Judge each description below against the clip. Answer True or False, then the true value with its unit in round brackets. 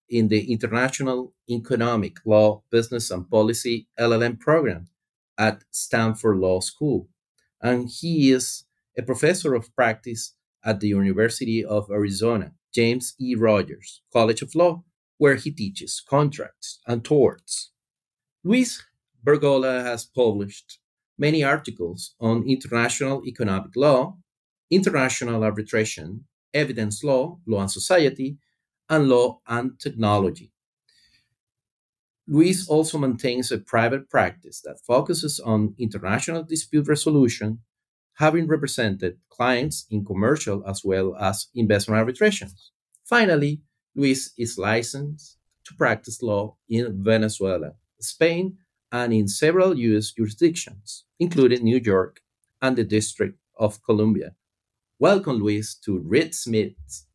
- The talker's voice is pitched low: True (120 Hz)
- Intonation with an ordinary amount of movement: True (4.5 semitones)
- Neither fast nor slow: False (115 wpm)